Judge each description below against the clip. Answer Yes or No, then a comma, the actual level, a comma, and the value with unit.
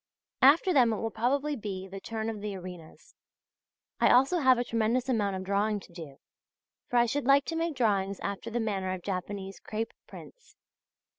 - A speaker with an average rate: Yes, average, 190 wpm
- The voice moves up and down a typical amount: Yes, average, 4.7 semitones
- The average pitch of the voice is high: Yes, high, 220 Hz